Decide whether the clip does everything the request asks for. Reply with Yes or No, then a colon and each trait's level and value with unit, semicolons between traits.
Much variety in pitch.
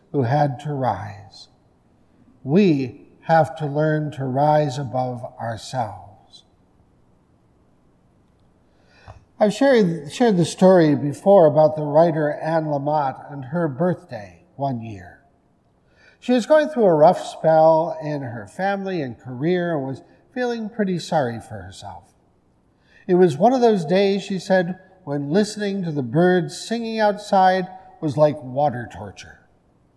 Yes: wide, 6.3 semitones